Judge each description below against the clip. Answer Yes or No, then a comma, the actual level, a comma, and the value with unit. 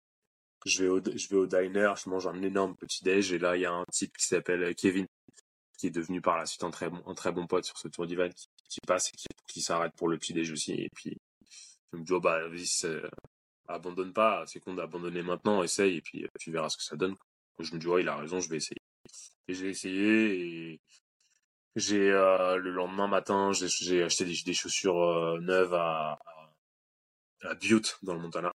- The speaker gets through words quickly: Yes, fast, 225 wpm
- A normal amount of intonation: No, narrow, 1.8 semitones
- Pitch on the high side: No, very low, 90 Hz